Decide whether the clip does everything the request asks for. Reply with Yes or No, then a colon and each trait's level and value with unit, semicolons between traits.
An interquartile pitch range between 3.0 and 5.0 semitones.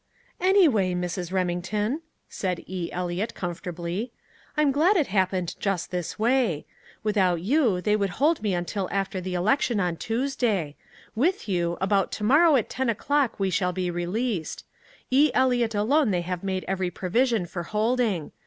No: wide, 5.6 semitones